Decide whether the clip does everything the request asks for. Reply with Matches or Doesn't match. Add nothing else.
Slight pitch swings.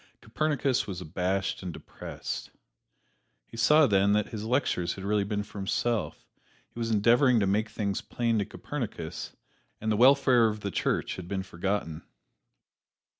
Doesn't match